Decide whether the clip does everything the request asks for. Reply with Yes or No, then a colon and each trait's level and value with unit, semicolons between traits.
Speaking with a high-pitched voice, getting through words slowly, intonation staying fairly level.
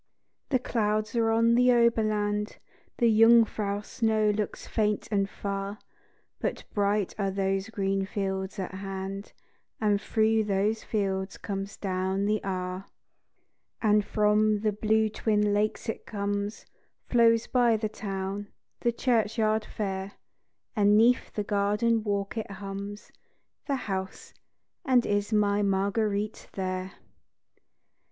Yes: high, 210 Hz; slow, 130 wpm; narrow, 1.9 semitones